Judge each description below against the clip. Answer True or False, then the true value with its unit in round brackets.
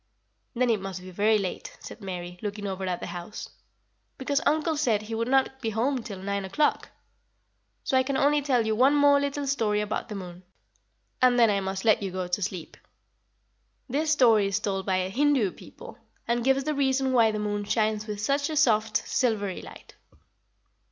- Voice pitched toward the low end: False (220 Hz)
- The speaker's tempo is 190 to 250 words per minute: True (195 wpm)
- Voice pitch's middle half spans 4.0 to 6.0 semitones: True (5.1 semitones)